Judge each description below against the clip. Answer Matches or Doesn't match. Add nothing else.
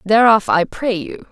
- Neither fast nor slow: Matches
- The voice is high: Matches